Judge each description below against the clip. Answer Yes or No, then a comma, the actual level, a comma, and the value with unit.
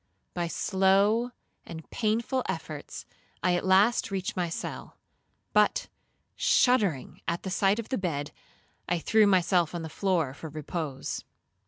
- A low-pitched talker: No, medium, 185 Hz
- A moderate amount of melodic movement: Yes, average, 3.7 semitones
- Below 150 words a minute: Yes, average, 140 wpm